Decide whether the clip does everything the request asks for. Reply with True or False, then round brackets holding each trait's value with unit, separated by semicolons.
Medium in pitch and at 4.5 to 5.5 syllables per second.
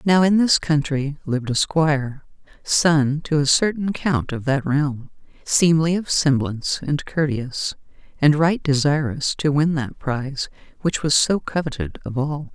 False (150 Hz; 4.3 syllables/s)